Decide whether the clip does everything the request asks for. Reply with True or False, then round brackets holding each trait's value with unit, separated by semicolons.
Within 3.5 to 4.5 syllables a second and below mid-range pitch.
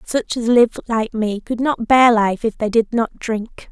False (4.0 syllables/s; 225 Hz)